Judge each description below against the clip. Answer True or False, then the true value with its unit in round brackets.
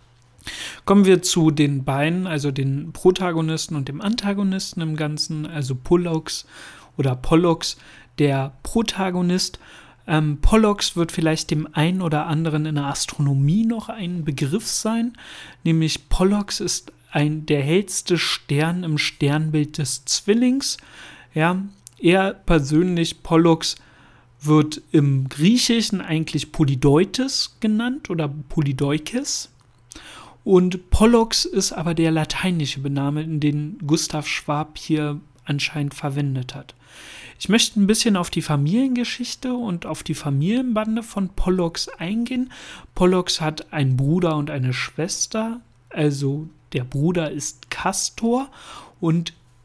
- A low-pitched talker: False (160 Hz)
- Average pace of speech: False (120 wpm)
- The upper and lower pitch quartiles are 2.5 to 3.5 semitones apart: False (4.4 semitones)